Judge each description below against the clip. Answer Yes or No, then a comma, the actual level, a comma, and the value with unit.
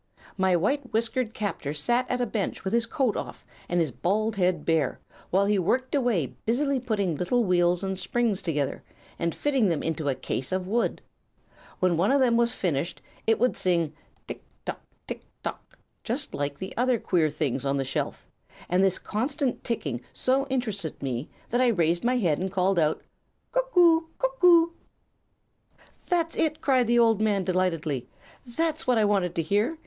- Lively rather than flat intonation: Yes, wide, 6.5 semitones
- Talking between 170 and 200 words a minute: Yes, average, 180 wpm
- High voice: Yes, high, 205 Hz